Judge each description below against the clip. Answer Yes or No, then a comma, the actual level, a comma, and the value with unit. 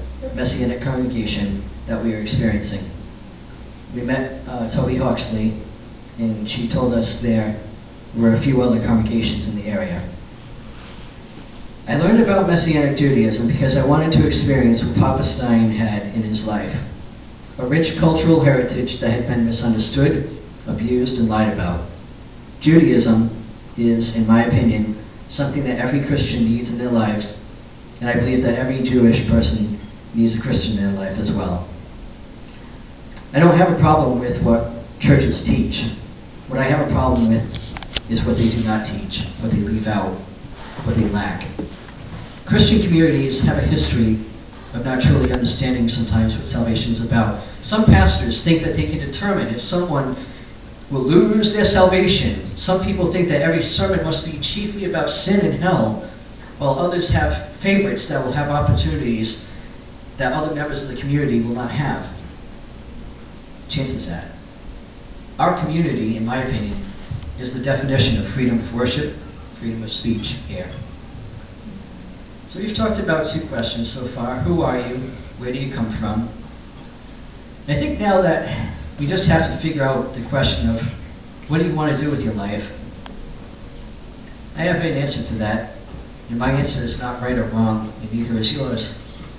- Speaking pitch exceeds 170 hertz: No, low, 120 Hz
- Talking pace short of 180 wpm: Yes, average, 160 wpm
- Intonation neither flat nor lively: Yes, average, 3.9 semitones